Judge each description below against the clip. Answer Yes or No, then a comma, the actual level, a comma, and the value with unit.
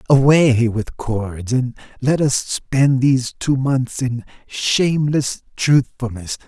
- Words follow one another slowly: Yes, slow, 120 wpm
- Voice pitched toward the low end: Yes, low, 130 Hz